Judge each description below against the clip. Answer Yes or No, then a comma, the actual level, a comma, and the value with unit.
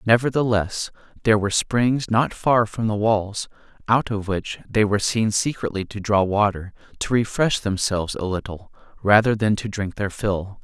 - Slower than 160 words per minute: No, average, 170 wpm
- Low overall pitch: Yes, low, 105 Hz